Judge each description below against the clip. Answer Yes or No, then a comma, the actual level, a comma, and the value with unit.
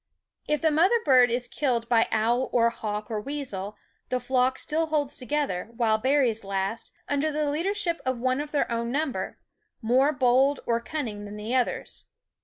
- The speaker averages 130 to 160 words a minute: No, average, 175 wpm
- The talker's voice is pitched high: Yes, very high, 255 Hz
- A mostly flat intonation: No, average, 4.1 semitones